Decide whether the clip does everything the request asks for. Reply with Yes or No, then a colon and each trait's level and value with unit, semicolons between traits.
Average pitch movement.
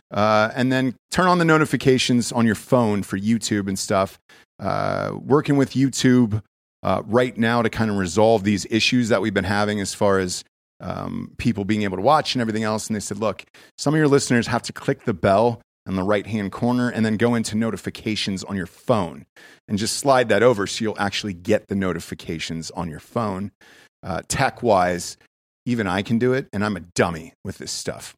Yes: average, 3.5 semitones